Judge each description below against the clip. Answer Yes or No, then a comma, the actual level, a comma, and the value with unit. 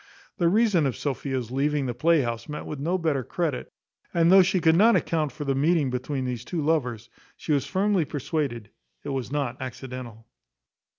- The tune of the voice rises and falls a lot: No, average, 4.5 semitones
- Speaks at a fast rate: No, average, 180 wpm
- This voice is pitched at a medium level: Yes, medium, 145 Hz